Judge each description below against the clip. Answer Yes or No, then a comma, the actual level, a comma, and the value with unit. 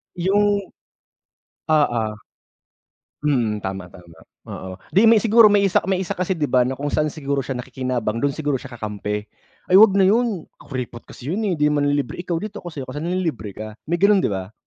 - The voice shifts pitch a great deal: Yes, wide, 7.6 semitones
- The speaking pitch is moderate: Yes, medium, 145 Hz